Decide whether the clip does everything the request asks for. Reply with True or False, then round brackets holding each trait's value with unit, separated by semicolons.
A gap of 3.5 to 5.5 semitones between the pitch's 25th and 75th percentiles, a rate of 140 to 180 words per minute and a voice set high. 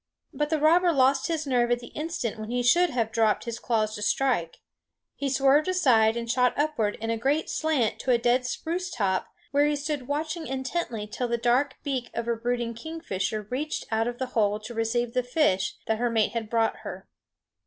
False (4.3 semitones; 205 wpm; 245 Hz)